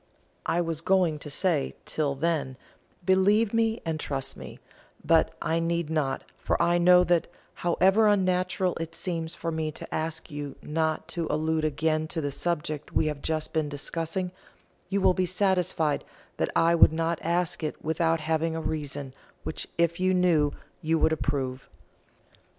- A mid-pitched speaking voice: Yes, medium, 165 Hz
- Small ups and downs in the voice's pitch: Yes, narrow, 2.3 semitones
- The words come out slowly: No, average, 165 wpm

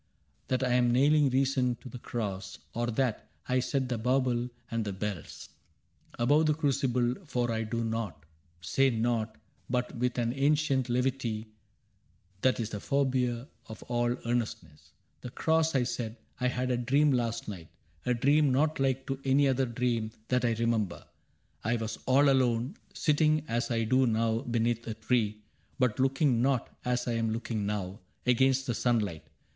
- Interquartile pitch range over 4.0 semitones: No, narrow, 2.6 semitones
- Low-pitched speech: Yes, low, 120 Hz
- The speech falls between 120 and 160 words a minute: No, average, 170 wpm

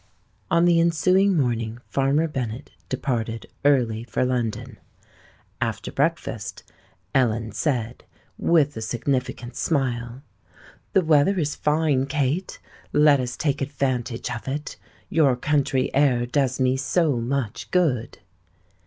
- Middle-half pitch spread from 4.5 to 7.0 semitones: No, average, 3.7 semitones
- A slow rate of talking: Yes, slow, 120 wpm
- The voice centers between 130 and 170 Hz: Yes, low, 135 Hz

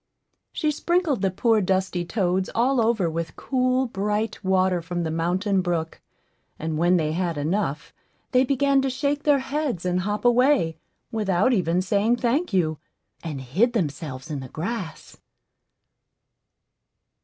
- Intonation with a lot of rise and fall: Yes, wide, 6.3 semitones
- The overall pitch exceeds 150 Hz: Yes, high, 190 Hz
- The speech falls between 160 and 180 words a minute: No, average, 145 wpm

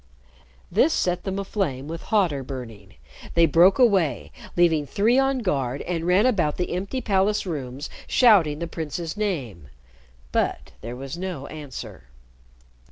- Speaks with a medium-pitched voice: Yes, medium, 170 Hz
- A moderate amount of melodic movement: No, wide, 6.1 semitones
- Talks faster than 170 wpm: No, average, 140 wpm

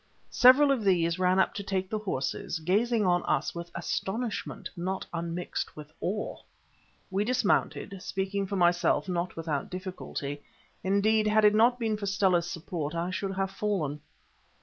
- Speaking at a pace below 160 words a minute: Yes, average, 150 wpm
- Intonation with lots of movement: No, average, 3.4 semitones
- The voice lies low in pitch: No, high, 190 Hz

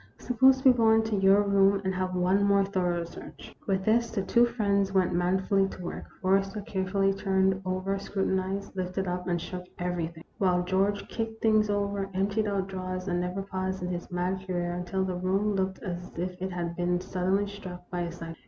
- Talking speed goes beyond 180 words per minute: Yes, average, 200 wpm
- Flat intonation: Yes, narrow, 1.8 semitones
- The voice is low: No, high, 190 Hz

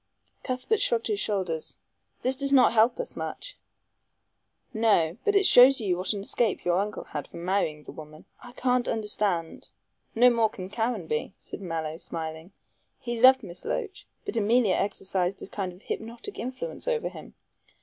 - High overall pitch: Yes, high, 210 Hz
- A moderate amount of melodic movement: No, wide, 5.7 semitones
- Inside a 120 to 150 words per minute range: No, average, 170 wpm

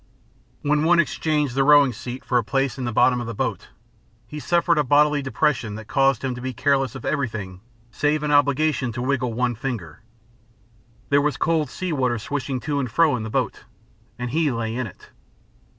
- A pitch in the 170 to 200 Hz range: No, low, 135 Hz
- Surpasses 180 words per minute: Yes, average, 200 wpm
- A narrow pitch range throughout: No, average, 3.4 semitones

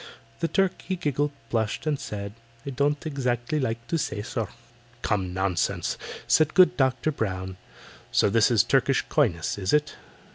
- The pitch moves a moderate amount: No, wide, 6.2 semitones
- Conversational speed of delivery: Yes, average, 155 wpm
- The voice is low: Yes, low, 125 Hz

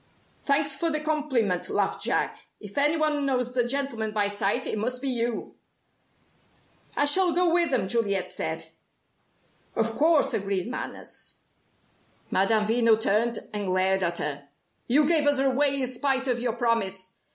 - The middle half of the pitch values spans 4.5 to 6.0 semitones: Yes, wide, 5.5 semitones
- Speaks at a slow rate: No, average, 155 wpm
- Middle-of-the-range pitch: No, high, 240 Hz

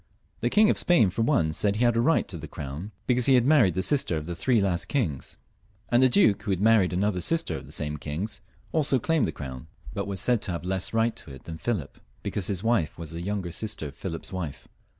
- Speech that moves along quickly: Yes, fast, 250 wpm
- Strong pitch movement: Yes, wide, 6.1 semitones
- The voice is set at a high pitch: No, low, 100 Hz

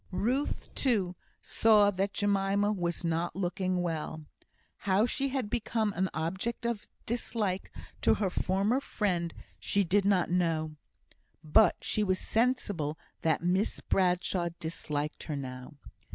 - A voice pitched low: No, high, 190 Hz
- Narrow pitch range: No, average, 3.6 semitones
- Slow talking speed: Yes, slow, 130 wpm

